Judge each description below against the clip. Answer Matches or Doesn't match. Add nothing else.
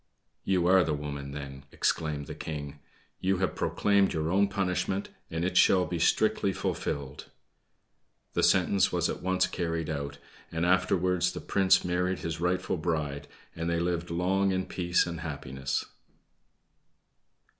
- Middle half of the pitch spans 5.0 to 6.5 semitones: Doesn't match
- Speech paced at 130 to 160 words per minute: Matches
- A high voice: Doesn't match